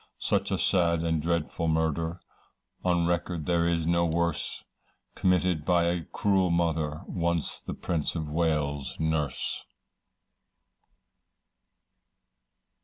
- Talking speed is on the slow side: Yes, slow, 110 wpm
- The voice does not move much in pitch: Yes, narrow, 1.4 semitones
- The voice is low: Yes, very low, 85 Hz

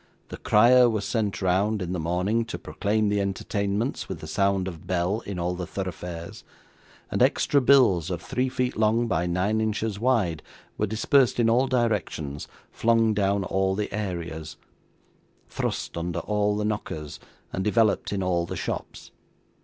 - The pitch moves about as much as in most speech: Yes, average, 3.7 semitones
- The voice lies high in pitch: No, low, 100 Hz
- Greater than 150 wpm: Yes, average, 160 wpm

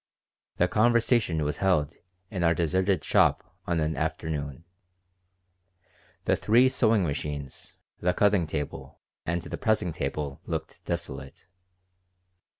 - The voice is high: No, very low, 85 Hz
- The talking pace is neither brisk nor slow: No, slow, 115 wpm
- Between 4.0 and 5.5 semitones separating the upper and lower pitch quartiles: Yes, average, 4.6 semitones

